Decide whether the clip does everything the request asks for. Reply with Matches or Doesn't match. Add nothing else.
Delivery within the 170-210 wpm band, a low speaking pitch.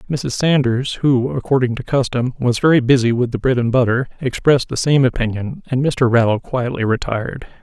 Matches